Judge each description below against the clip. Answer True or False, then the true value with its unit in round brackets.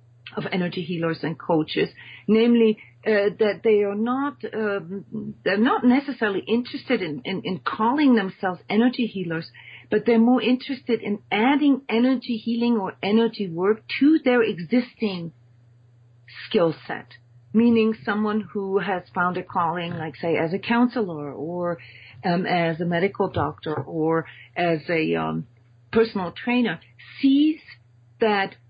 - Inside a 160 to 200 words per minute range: False (135 wpm)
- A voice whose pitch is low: False (195 Hz)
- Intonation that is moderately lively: False (5.9 semitones)